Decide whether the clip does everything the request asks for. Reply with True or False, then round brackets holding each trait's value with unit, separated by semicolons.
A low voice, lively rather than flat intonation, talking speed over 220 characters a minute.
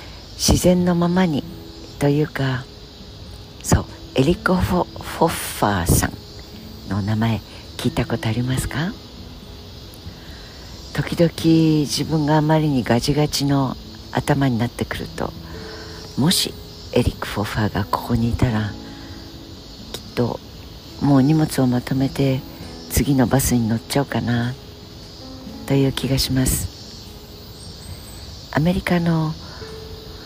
True (115 Hz; 6.2 semitones; 235 characters per minute)